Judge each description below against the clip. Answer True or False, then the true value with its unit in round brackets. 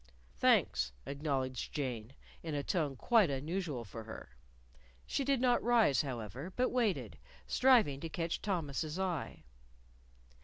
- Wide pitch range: True (6.9 semitones)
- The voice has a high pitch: False (155 Hz)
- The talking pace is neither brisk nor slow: False (125 wpm)